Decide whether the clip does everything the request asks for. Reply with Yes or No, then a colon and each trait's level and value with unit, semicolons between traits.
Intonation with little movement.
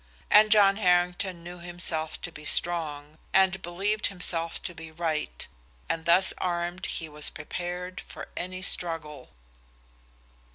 Yes: narrow, 2.2 semitones